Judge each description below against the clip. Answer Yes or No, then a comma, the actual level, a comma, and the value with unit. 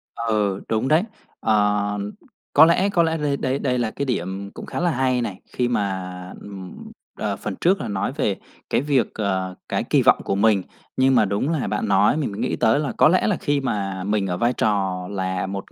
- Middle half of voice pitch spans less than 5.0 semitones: No, wide, 5.6 semitones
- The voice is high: No, low, 110 Hz